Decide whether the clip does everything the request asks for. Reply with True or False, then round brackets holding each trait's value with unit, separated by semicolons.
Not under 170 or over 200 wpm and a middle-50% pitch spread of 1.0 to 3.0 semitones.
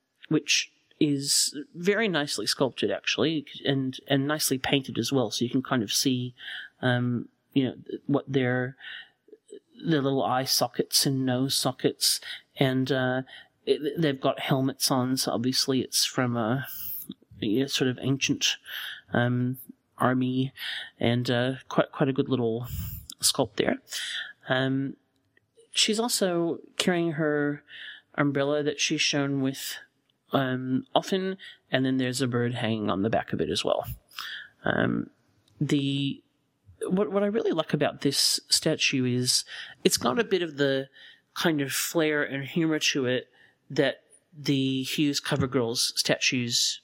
False (145 wpm; 2.7 semitones)